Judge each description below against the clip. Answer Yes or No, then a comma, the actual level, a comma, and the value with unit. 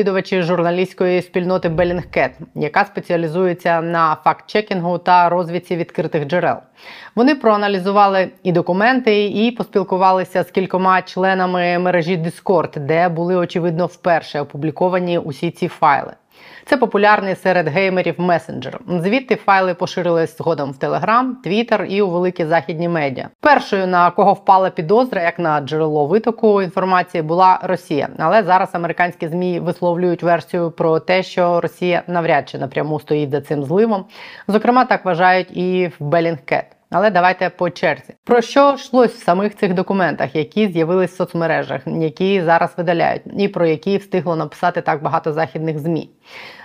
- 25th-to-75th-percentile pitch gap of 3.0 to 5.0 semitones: No, narrow, 2.5 semitones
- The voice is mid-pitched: Yes, medium, 180 Hz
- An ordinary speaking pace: Yes, average, 145 wpm